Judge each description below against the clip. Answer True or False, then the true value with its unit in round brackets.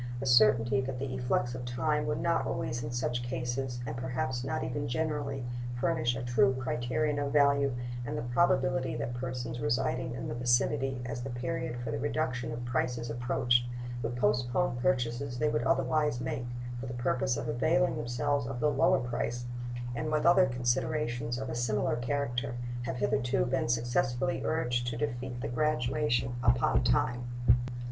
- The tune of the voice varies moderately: False (1.7 semitones)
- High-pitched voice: False (125 Hz)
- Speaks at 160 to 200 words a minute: True (165 wpm)